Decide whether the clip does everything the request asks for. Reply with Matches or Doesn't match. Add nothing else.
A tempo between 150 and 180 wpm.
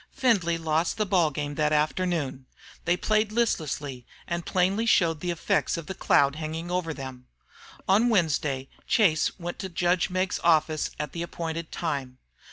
Matches